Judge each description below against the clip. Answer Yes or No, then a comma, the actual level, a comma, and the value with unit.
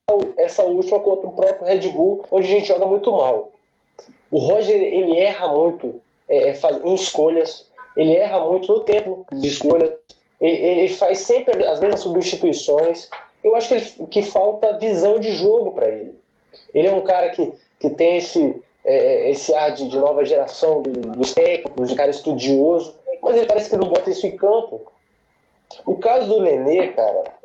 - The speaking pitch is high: Yes, high, 210 Hz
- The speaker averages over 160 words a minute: Yes, average, 180 wpm